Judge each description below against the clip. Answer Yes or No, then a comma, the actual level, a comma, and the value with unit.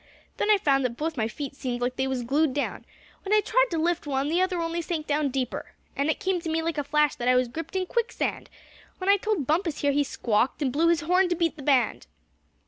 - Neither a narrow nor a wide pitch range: Yes, average, 4.3 semitones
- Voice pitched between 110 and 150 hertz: No, very high, 305 Hz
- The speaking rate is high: Yes, fast, 255 wpm